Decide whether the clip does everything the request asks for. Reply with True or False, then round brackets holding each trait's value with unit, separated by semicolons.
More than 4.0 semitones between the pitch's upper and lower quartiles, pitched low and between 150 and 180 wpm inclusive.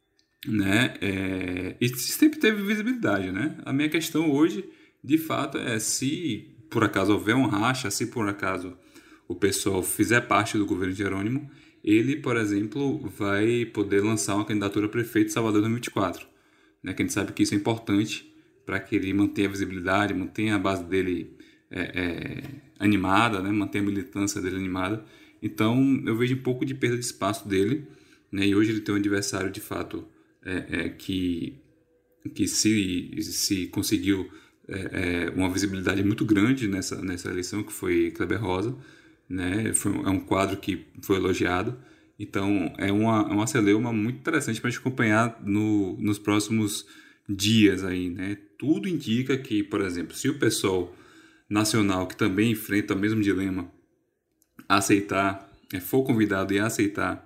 False (3.5 semitones; 105 Hz; 160 wpm)